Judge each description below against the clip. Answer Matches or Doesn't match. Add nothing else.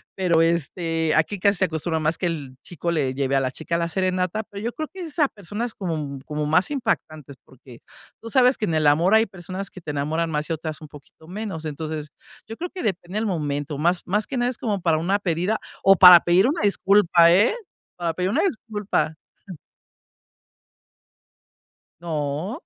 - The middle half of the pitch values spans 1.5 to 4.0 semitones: Doesn't match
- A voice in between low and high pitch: Matches